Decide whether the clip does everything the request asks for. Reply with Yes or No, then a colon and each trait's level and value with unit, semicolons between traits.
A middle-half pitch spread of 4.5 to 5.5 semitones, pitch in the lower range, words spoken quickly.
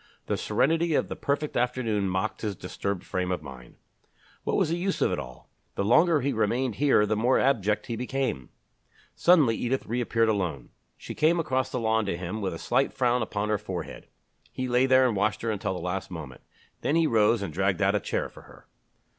Yes: average, 5.1 semitones; low, 110 Hz; fast, 210 wpm